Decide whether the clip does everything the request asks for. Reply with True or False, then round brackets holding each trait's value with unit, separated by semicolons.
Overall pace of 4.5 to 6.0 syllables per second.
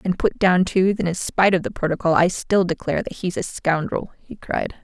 True (5.4 syllables/s)